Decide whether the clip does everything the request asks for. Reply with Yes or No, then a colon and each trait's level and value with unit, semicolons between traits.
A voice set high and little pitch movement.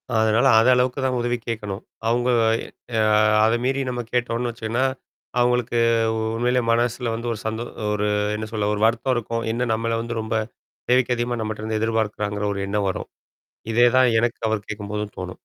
No: low, 115 Hz; narrow, 2.1 semitones